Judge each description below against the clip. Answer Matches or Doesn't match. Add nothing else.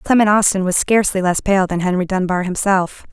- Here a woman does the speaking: Matches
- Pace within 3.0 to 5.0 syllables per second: Doesn't match